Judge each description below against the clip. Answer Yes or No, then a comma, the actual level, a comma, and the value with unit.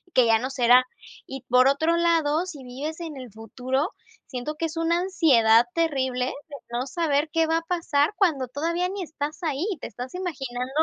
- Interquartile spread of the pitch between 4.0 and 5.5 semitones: Yes, average, 4.5 semitones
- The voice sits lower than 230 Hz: No, very high, 290 Hz